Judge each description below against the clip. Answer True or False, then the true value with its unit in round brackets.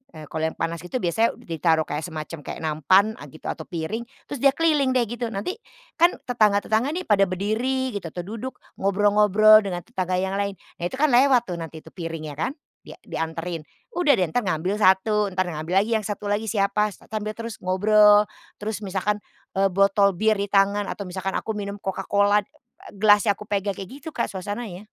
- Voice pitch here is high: True (200 Hz)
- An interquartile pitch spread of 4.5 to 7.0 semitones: False (3.1 semitones)